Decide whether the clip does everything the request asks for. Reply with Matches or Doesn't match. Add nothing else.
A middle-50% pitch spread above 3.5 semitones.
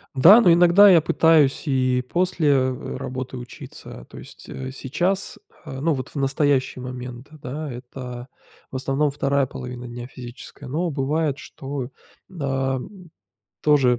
Doesn't match